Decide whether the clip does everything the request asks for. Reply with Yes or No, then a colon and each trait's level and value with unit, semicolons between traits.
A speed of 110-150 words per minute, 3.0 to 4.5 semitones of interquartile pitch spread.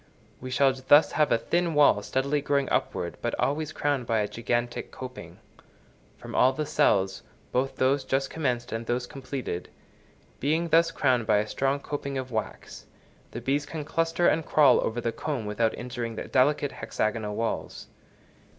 No: average, 170 wpm; average, 3.7 semitones